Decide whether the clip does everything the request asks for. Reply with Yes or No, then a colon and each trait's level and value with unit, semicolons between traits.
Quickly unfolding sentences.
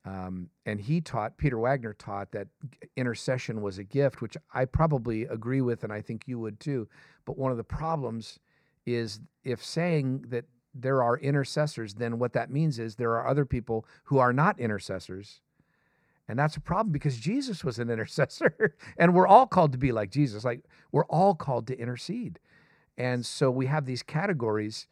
No: average, 185 wpm